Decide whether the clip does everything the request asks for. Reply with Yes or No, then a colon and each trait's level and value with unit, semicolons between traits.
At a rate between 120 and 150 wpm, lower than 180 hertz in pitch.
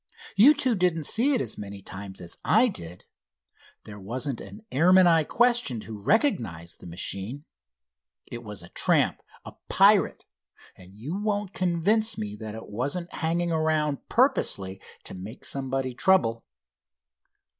Yes: average, 145 wpm; medium, 140 Hz